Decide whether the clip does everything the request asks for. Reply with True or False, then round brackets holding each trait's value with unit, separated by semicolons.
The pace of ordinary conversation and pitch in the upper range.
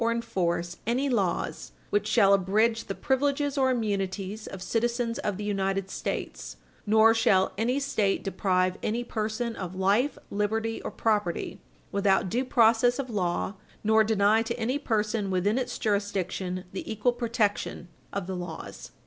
True (150 wpm; 215 Hz)